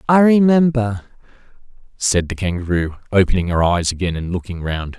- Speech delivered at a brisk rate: No, average, 145 wpm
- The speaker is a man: Yes, male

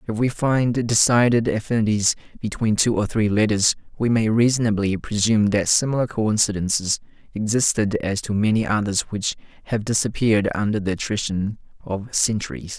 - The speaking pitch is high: No, low, 110 Hz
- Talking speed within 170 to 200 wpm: No, average, 140 wpm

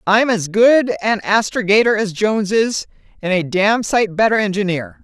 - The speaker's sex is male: No, female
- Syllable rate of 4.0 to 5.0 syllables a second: Yes, 4.6 syllables/s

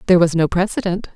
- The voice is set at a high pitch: No, medium, 175 Hz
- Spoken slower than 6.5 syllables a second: No, 7.2 syllables/s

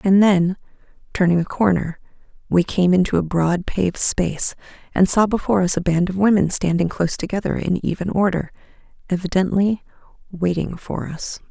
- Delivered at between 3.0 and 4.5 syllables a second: No, 5.4 syllables/s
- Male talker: No, female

